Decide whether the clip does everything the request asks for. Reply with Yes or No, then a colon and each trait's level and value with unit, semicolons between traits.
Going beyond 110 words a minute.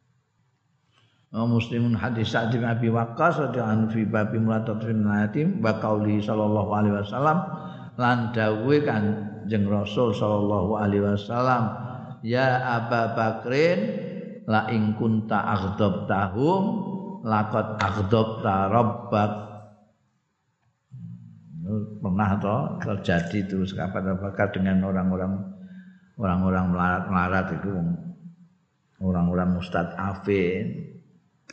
No: average, 95 wpm